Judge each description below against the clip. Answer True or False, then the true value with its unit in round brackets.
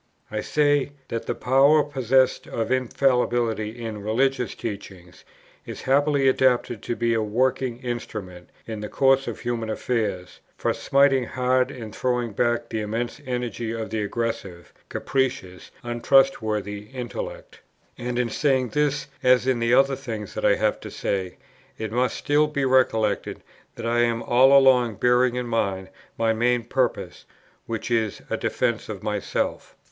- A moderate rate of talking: True (150 wpm)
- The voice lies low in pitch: True (120 Hz)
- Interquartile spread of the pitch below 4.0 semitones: True (3.0 semitones)